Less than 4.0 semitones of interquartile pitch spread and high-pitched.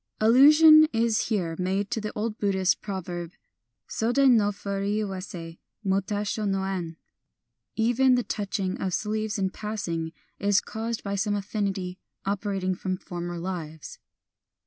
Yes: average, 2.7 semitones; high, 200 Hz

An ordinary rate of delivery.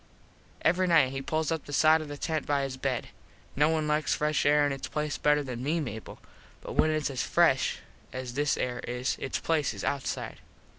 No: fast, 210 wpm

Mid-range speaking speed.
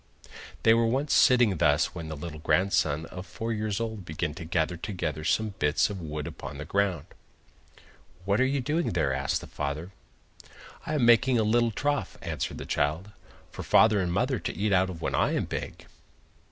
Yes: average, 195 wpm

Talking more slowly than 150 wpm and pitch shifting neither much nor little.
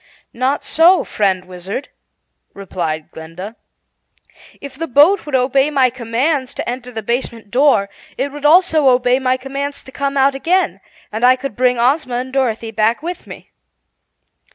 No: average, 155 wpm; average, 3.6 semitones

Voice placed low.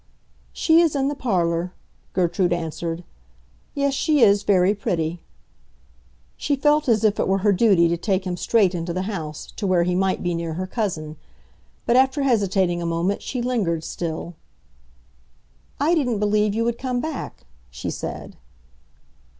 No: high, 195 Hz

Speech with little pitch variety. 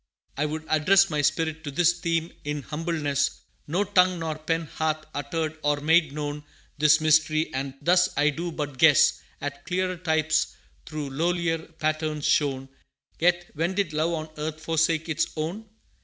Yes: narrow, 2.1 semitones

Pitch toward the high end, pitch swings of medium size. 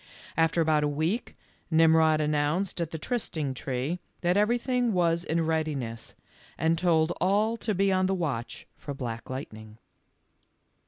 No: medium, 160 Hz; average, 3.9 semitones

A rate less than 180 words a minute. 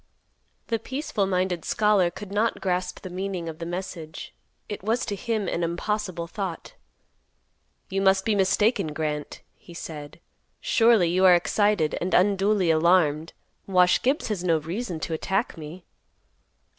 Yes: average, 145 wpm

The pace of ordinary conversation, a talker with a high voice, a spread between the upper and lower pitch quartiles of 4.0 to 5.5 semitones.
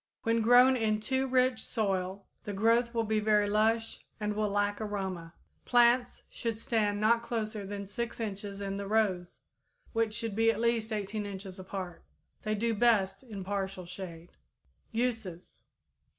No: average, 155 wpm; high, 215 Hz; narrow, 2.5 semitones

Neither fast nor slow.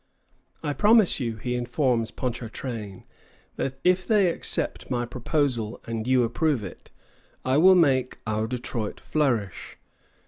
No: slow, 130 wpm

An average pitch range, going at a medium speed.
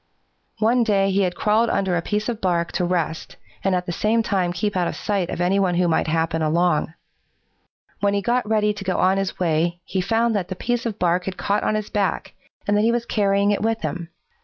No: average, 3.1 semitones; fast, 235 wpm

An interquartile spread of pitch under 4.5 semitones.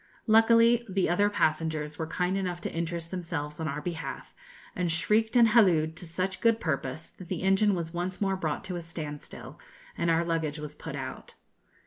Yes: average, 3.1 semitones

